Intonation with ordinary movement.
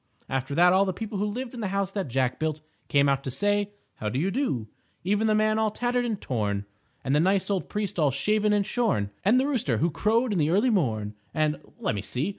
No: wide, 7.6 semitones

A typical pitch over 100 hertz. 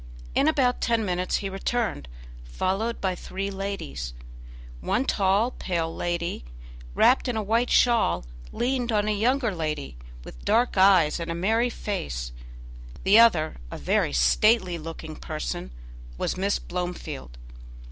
Yes: high, 190 Hz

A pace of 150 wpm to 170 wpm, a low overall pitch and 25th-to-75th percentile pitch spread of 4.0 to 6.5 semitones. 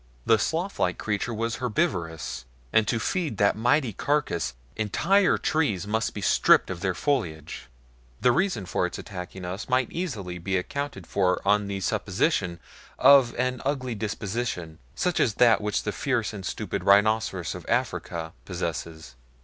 Yes: average, 155 wpm; low, 105 Hz; wide, 5.6 semitones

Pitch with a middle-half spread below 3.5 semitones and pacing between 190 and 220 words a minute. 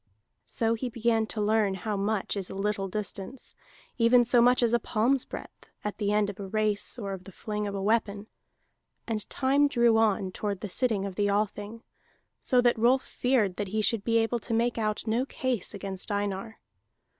Yes: narrow, 2.6 semitones; average, 200 wpm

